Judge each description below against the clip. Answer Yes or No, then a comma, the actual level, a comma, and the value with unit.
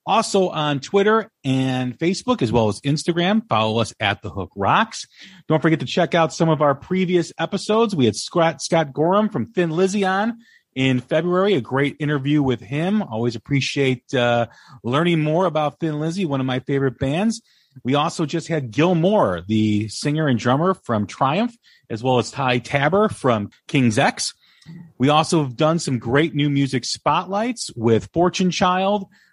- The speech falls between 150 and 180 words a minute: Yes, average, 175 wpm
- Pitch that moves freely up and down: Yes, wide, 6.0 semitones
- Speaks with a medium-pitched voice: Yes, medium, 150 Hz